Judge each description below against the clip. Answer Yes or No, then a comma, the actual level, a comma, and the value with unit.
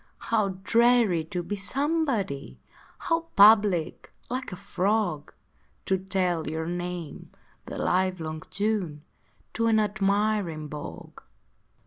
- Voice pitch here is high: Yes, high, 195 Hz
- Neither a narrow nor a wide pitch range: Yes, average, 4.2 semitones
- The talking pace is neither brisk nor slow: No, slow, 105 wpm